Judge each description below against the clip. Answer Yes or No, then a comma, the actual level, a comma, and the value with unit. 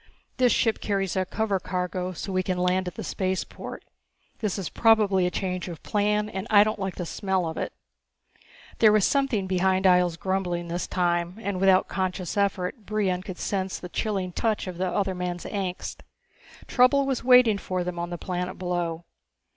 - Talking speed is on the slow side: No, average, 185 wpm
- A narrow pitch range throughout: Yes, narrow, 2.3 semitones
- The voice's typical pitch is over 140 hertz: Yes, high, 190 Hz